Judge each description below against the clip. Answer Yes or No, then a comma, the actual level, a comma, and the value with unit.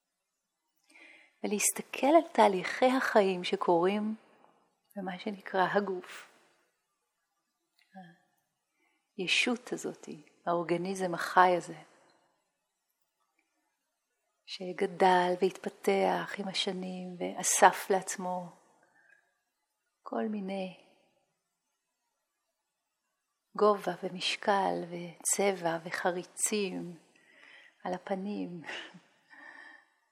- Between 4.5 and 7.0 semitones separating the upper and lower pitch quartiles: No, average, 2.7 semitones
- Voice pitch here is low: No, high, 195 Hz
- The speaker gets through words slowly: Yes, slow, 55 wpm